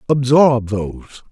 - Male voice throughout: Yes, male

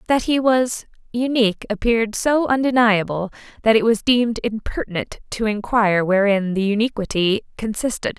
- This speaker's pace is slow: Yes, slow, 130 wpm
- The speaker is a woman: Yes, female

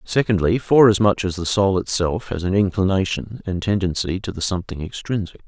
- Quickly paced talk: No, average, 165 wpm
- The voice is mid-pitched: No, very low, 95 Hz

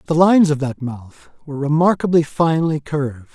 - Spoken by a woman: No, male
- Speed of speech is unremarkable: Yes, average, 160 wpm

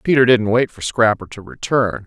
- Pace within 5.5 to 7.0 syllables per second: No, 5.1 syllables/s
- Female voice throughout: No, male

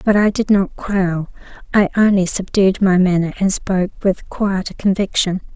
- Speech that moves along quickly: No, average, 160 wpm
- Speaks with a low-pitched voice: No, high, 190 Hz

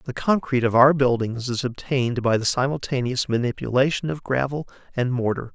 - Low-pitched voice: Yes, low, 130 Hz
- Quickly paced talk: No, average, 160 wpm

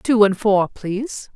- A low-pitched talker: No, high, 210 Hz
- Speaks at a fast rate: No, average, 175 wpm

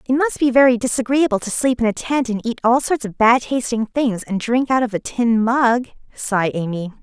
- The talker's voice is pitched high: Yes, high, 235 Hz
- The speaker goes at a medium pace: No, fast, 230 wpm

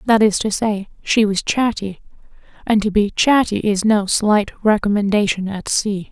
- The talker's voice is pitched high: Yes, high, 210 Hz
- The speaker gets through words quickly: No, average, 165 wpm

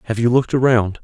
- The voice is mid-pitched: No, low, 120 Hz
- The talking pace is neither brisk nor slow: No, fast, 235 wpm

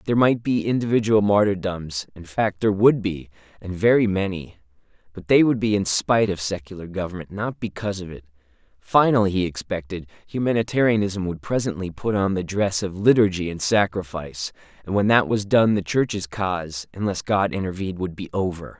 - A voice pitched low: Yes, low, 100 Hz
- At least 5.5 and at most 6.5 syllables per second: Yes, 5.6 syllables/s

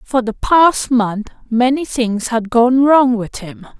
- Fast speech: No, average, 175 wpm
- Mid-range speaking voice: No, high, 240 Hz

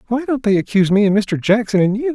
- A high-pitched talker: Yes, high, 215 Hz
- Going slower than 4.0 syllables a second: No, 6.4 syllables/s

